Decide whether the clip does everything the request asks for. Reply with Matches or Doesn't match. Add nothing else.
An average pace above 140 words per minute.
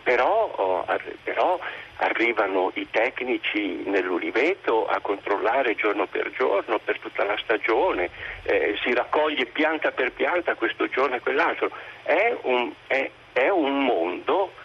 Doesn't match